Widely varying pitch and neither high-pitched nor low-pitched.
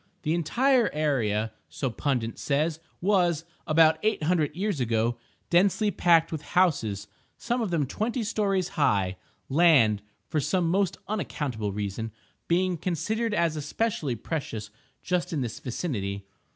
Yes: wide, 7.6 semitones; medium, 155 Hz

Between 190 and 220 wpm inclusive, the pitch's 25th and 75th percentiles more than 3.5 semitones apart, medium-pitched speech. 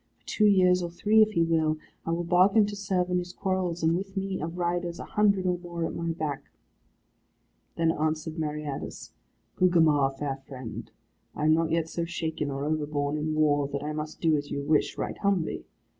No: average, 200 wpm; average, 2.9 semitones; medium, 165 Hz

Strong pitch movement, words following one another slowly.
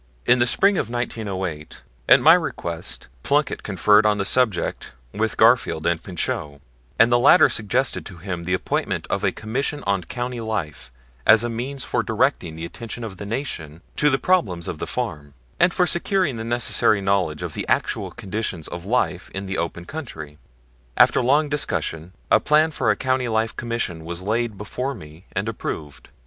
No: wide, 6.2 semitones; average, 180 wpm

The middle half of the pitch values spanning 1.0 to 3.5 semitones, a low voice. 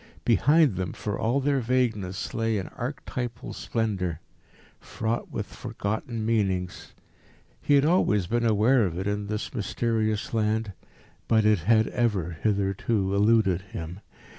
Yes: average, 3.2 semitones; low, 110 Hz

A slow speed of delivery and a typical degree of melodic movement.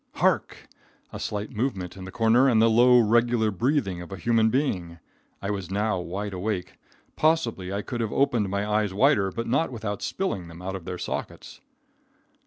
No: average, 185 wpm; average, 3.8 semitones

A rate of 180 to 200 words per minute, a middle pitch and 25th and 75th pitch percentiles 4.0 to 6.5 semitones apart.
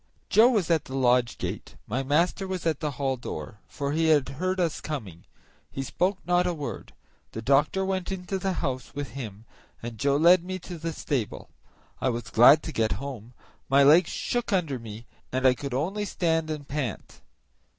Yes: average, 190 wpm; medium, 145 Hz; wide, 5.6 semitones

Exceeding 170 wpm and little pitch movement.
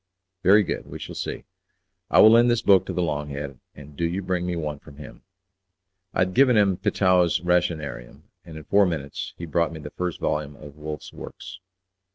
No: fast, 205 wpm; average, 4.0 semitones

